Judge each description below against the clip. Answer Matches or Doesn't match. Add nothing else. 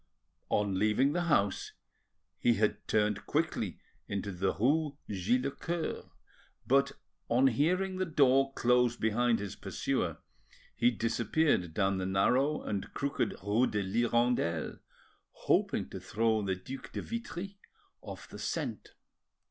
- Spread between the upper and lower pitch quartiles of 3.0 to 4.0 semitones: Doesn't match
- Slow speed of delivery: Matches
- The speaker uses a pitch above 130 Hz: Doesn't match